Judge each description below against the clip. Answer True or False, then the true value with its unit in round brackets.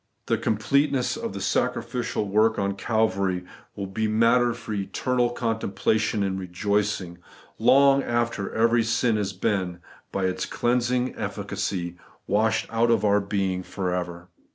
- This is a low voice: True (110 Hz)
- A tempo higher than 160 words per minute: False (140 wpm)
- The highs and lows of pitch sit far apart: False (3.4 semitones)